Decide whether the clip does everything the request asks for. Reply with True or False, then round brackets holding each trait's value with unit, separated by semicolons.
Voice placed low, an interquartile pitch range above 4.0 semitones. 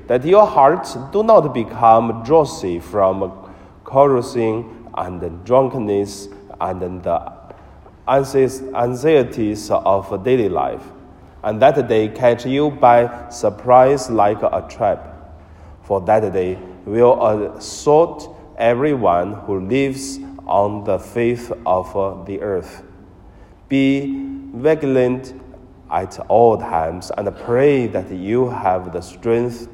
True (115 Hz; 5.4 semitones)